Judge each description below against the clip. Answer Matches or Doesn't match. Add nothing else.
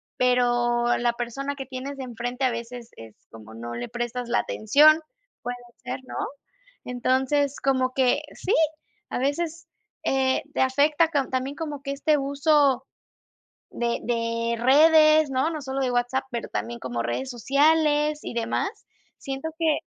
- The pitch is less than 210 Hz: Doesn't match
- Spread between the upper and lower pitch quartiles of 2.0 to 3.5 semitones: Matches